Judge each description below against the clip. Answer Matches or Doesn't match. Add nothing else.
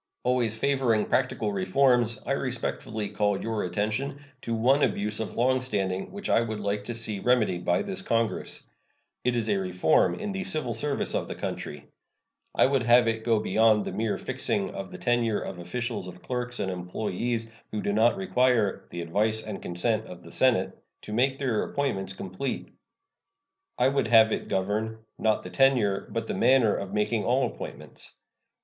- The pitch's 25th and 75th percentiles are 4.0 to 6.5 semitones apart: Doesn't match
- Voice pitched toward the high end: Doesn't match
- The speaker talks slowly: Doesn't match